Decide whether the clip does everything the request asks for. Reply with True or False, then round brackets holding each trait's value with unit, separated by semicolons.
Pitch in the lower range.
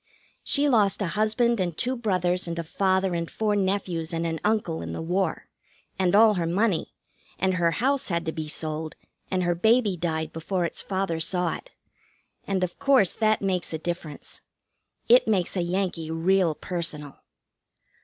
False (180 Hz)